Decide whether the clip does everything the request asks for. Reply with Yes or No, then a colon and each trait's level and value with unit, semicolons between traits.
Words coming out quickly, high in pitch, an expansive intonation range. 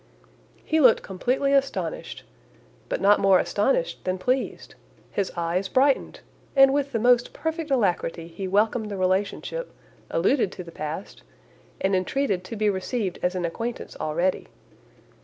No: average, 140 wpm; high, 205 Hz; wide, 6.3 semitones